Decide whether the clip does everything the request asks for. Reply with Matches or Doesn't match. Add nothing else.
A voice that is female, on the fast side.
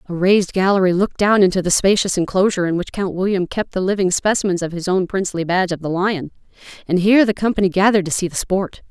Matches